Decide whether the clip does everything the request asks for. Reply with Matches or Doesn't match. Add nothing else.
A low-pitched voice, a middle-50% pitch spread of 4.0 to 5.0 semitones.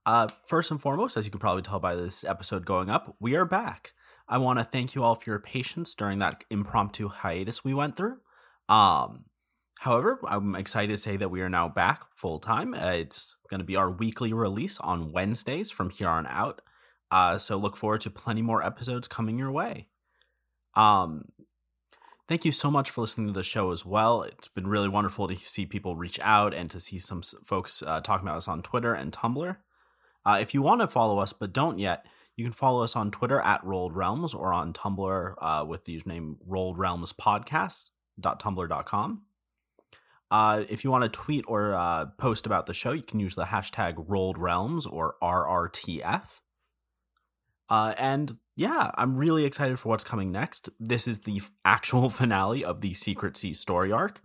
Matches